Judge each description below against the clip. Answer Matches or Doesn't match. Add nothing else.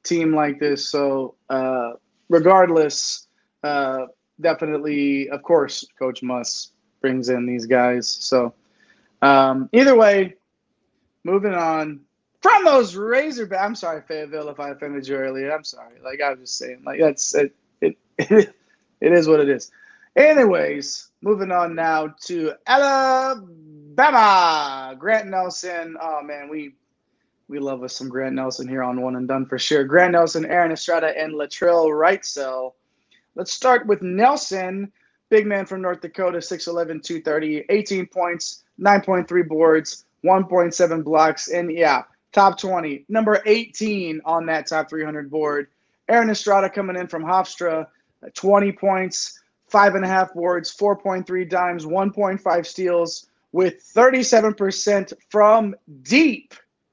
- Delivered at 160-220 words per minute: Doesn't match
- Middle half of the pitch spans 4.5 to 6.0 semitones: Matches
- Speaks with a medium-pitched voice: Matches